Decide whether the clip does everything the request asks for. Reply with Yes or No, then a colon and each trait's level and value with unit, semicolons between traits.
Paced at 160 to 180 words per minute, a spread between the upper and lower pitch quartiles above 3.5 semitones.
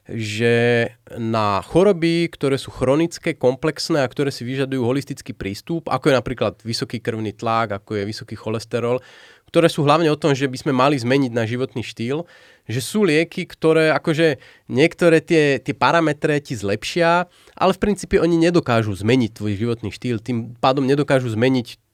Yes: fast, 165 wpm; wide, 5.4 semitones